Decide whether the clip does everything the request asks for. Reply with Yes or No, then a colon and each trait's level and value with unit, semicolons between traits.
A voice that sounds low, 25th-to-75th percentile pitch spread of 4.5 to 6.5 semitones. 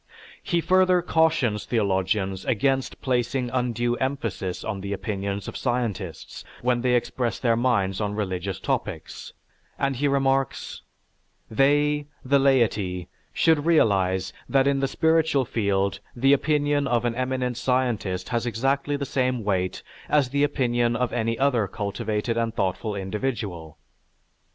Yes: low, 120 Hz; average, 5.0 semitones